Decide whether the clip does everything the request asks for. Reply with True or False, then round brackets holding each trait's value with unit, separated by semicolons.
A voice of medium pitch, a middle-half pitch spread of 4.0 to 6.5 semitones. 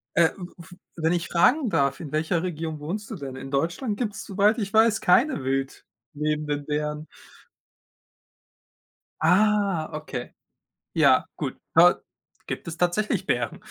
True (170 Hz; 5.3 semitones)